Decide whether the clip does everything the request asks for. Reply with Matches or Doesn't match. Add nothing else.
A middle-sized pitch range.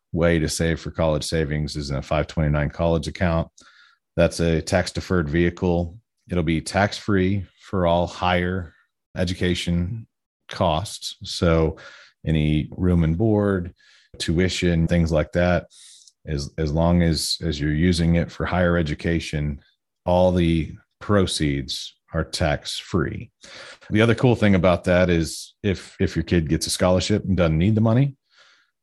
Doesn't match